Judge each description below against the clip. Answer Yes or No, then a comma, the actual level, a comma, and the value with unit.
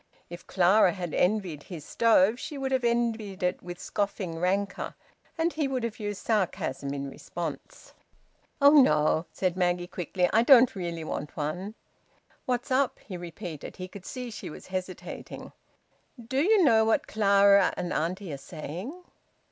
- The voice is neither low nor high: No, high, 195 Hz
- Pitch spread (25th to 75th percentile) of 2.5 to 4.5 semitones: No, average, 5.0 semitones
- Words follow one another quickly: No, average, 155 wpm